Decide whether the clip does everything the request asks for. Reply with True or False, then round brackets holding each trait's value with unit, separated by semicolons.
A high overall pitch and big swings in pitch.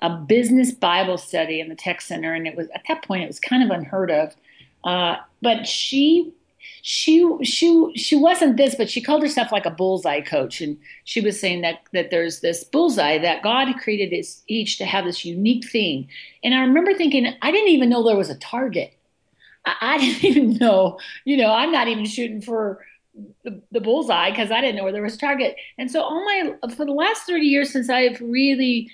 True (230 Hz; 6.8 semitones)